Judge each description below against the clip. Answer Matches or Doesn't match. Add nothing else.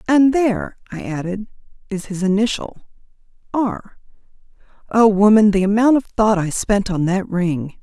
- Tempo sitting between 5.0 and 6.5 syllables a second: Doesn't match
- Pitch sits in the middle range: Doesn't match